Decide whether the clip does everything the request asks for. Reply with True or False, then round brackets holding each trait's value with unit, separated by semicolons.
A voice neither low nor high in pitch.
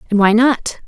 False (225 Hz)